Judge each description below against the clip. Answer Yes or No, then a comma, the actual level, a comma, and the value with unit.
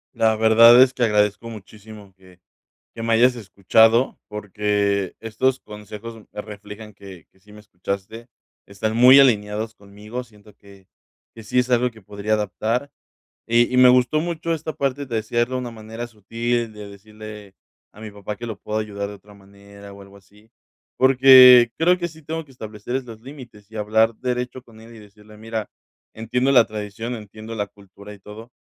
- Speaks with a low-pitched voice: Yes, low, 110 Hz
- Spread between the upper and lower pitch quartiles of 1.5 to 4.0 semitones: Yes, average, 2.8 semitones